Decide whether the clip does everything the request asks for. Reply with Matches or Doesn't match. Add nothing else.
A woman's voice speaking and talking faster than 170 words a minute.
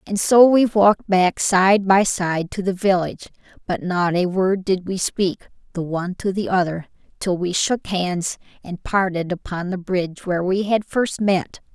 Matches